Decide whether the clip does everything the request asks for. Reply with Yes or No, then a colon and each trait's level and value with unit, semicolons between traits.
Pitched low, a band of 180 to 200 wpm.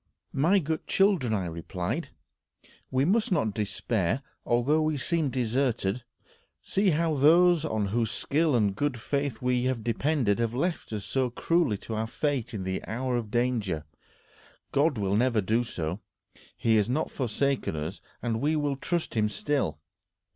No: low, 125 Hz; average, 155 wpm